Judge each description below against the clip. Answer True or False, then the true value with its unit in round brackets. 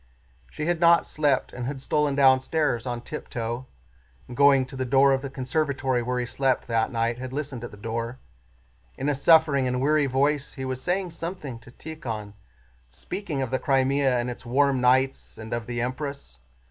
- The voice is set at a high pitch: False (130 Hz)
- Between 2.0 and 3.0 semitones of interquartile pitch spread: True (2.7 semitones)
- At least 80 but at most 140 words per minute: False (185 wpm)